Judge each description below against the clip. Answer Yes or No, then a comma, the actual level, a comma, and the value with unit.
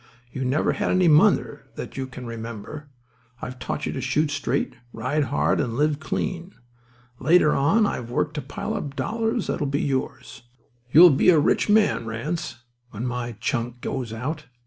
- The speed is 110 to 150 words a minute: No, average, 170 wpm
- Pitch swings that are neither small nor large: Yes, average, 4.1 semitones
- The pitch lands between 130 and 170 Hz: Yes, medium, 140 Hz